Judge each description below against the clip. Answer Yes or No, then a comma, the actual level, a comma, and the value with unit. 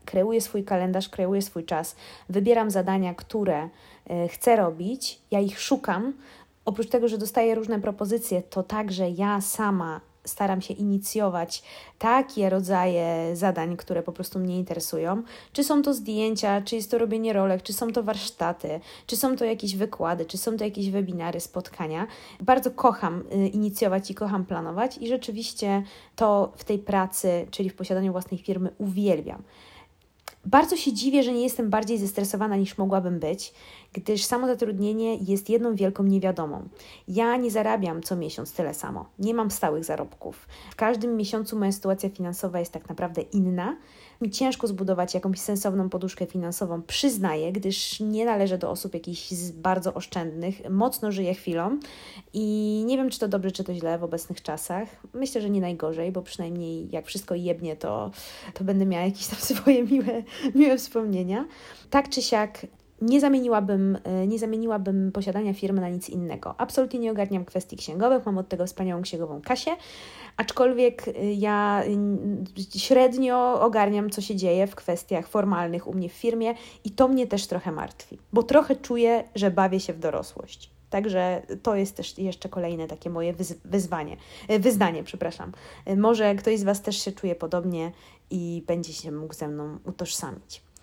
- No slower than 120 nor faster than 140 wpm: No, fast, 160 wpm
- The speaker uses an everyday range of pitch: Yes, average, 3.7 semitones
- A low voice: No, high, 200 Hz